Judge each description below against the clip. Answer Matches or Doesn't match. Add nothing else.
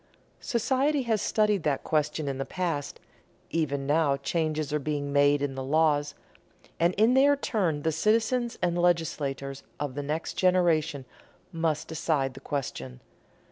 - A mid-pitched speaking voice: Matches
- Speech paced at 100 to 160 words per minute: Matches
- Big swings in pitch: Doesn't match